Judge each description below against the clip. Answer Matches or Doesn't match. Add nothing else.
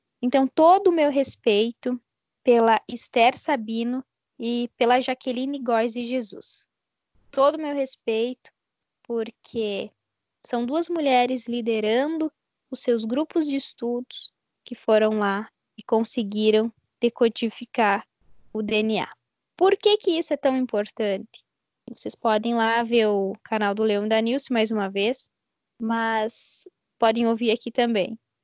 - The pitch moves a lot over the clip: Doesn't match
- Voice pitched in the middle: Doesn't match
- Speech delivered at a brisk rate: Doesn't match